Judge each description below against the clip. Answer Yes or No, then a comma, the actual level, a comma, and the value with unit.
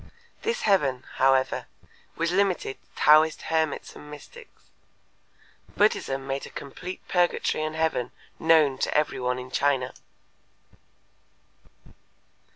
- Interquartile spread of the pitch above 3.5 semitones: Yes, average, 4.1 semitones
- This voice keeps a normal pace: No, slow, 110 wpm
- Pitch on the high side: No, medium, 150 Hz